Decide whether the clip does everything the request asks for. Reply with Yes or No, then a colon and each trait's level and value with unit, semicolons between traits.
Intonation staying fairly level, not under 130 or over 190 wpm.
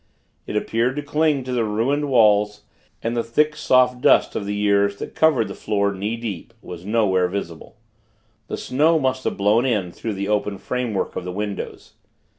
No: average, 4.0 semitones; average, 185 wpm